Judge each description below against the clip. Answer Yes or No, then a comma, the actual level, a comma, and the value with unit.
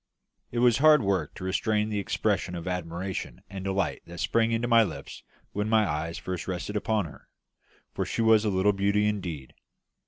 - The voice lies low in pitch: Yes, low, 100 Hz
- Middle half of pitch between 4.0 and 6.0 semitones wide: No, average, 3.3 semitones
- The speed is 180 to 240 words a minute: Yes, average, 185 wpm